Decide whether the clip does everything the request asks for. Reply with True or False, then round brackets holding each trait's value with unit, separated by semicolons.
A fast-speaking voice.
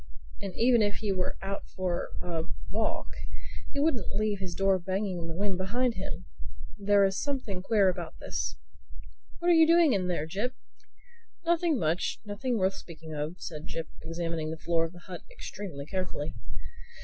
False (165 wpm)